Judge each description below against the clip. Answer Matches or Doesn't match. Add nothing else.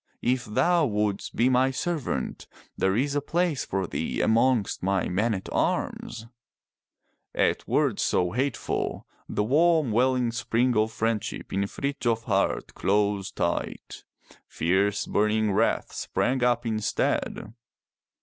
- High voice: Doesn't match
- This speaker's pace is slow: Matches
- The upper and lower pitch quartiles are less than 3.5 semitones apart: Doesn't match